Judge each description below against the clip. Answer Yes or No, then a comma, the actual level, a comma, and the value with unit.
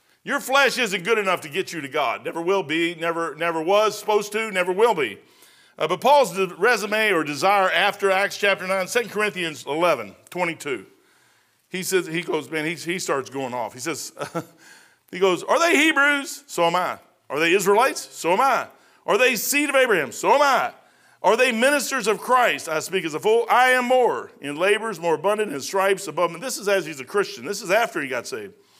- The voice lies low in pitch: No, high, 195 Hz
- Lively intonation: Yes, wide, 5.9 semitones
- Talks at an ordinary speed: No, fast, 215 wpm